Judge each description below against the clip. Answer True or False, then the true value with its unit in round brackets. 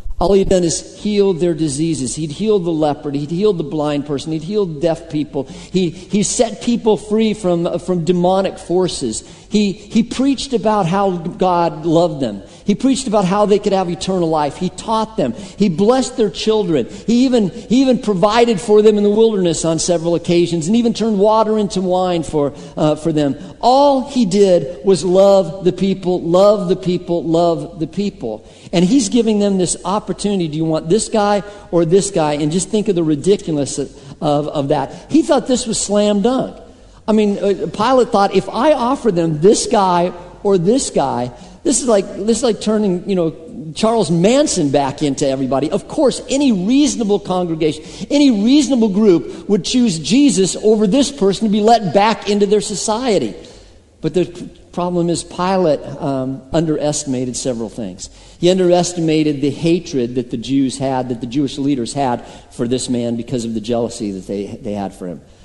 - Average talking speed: True (185 wpm)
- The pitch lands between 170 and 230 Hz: True (185 Hz)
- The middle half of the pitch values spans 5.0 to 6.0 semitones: True (5.3 semitones)